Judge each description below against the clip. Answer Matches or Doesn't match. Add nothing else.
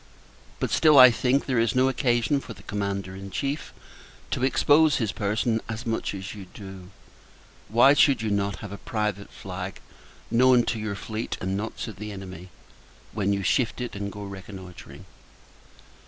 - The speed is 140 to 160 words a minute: Doesn't match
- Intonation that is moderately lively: Matches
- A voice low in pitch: Matches